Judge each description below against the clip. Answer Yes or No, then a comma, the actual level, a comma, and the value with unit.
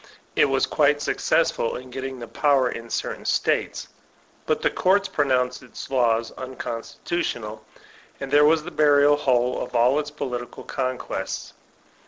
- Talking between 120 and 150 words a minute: Yes, average, 145 wpm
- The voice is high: No, low, 130 Hz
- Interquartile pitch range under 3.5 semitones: Yes, average, 3.0 semitones